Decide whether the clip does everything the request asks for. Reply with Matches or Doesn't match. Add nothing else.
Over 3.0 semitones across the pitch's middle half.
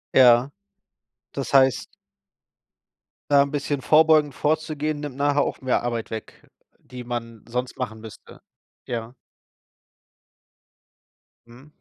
Matches